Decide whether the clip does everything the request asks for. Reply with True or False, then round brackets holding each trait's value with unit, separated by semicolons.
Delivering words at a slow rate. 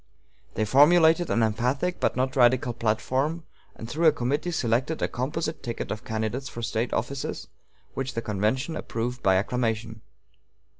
False (150 wpm)